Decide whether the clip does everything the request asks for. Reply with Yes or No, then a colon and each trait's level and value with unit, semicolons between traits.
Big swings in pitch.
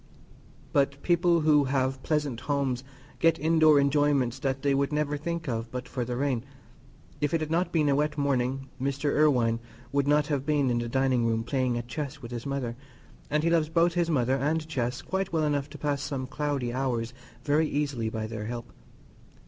No: average, 3.1 semitones